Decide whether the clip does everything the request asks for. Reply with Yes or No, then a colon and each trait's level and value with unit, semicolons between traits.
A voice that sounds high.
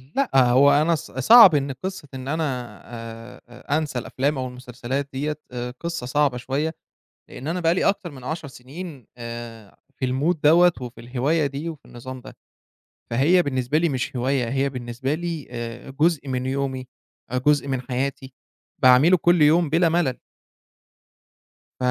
No: low, 135 Hz